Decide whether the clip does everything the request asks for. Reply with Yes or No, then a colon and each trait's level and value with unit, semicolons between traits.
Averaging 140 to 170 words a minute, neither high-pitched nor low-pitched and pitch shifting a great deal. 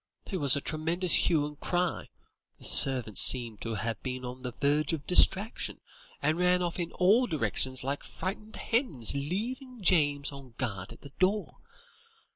Yes: average, 165 wpm; medium, 150 Hz; wide, 5.9 semitones